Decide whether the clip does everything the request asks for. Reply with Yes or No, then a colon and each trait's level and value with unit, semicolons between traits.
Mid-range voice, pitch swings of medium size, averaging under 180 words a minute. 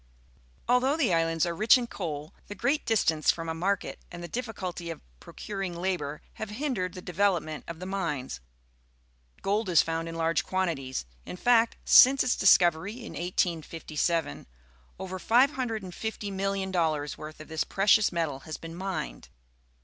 Yes: medium, 180 Hz; average, 4.1 semitones; average, 150 wpm